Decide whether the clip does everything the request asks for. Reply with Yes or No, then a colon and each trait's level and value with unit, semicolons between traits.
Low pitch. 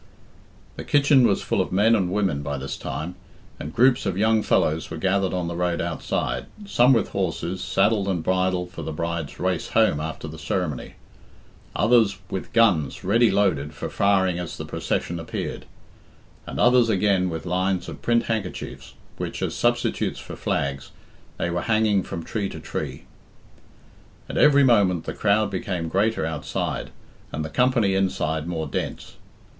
Yes: very low, 95 Hz